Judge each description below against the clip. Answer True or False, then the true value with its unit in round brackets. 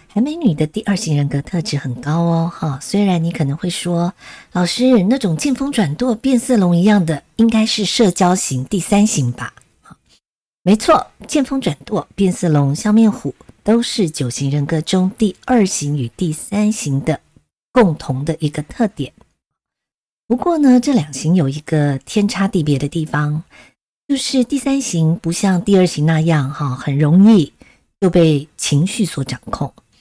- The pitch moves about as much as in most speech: False (6.1 semitones)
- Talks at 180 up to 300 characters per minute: True (240 characters per minute)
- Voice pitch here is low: False (175 Hz)